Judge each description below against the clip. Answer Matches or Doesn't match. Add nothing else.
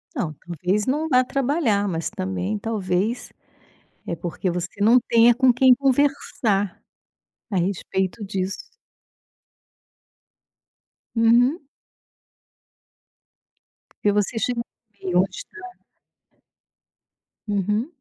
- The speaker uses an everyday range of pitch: Matches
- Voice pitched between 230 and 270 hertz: Doesn't match